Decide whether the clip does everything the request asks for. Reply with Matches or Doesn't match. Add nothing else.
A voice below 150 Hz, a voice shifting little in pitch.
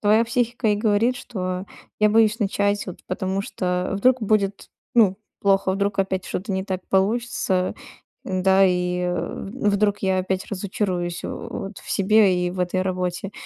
Doesn't match